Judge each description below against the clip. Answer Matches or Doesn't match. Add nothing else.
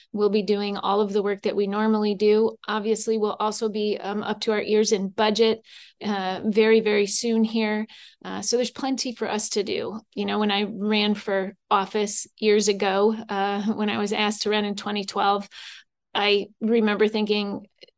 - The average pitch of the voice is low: Doesn't match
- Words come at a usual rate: Matches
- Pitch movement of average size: Doesn't match